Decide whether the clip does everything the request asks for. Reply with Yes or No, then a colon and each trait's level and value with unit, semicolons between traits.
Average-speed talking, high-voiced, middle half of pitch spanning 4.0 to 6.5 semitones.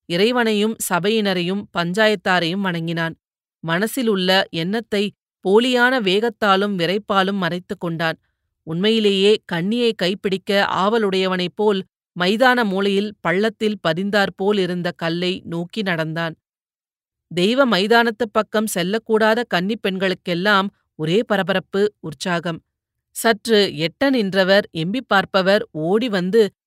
No: average, 90 wpm; high, 195 Hz; average, 3.5 semitones